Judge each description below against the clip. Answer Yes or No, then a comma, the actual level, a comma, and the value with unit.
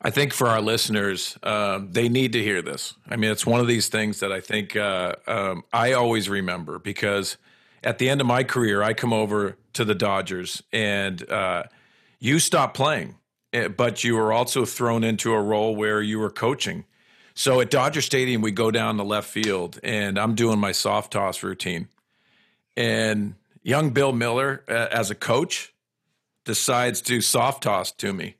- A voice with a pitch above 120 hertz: No, low, 110 Hz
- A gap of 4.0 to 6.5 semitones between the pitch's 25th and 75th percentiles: No, narrow, 2.5 semitones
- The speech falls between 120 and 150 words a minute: No, average, 185 wpm